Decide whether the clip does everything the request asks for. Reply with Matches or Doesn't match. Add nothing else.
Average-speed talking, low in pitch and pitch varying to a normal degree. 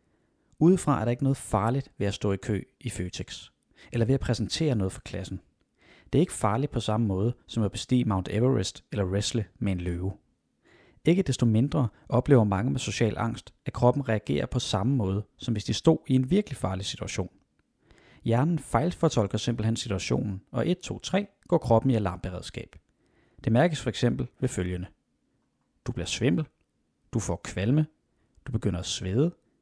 Matches